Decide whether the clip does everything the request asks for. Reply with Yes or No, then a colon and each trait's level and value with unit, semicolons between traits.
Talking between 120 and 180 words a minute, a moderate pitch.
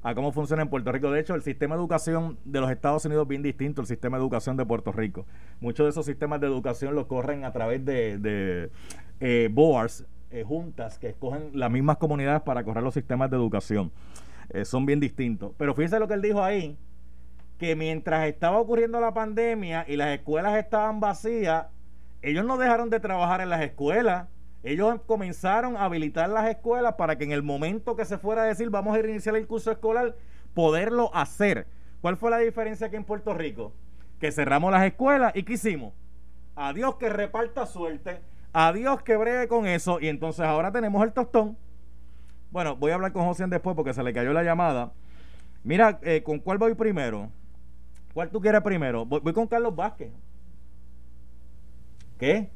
No: fast, 190 wpm; medium, 155 Hz